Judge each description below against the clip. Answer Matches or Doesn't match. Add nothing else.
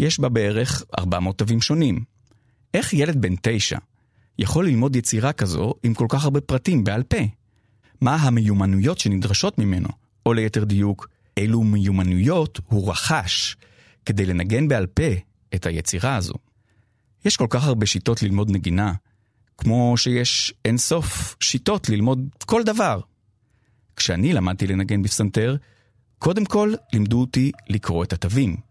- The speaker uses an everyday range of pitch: Matches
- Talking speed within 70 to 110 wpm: Doesn't match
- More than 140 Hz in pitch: Doesn't match